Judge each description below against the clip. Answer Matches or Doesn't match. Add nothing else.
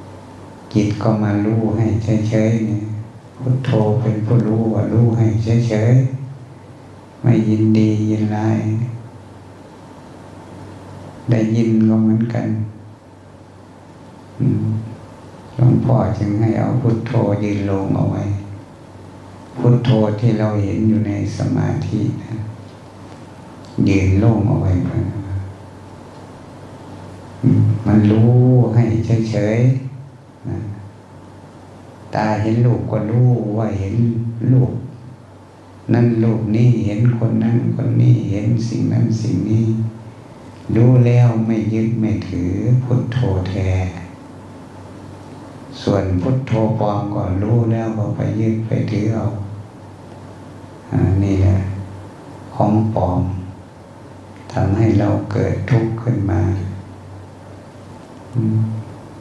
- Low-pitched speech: Matches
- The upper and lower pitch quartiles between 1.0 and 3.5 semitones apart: Matches